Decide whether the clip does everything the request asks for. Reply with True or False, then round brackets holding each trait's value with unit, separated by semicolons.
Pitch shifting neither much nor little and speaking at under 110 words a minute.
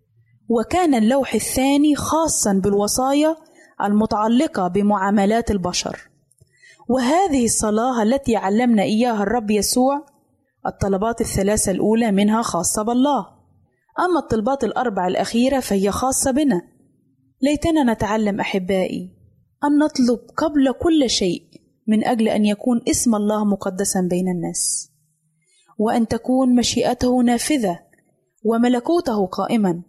True (4.7 semitones; 100 wpm)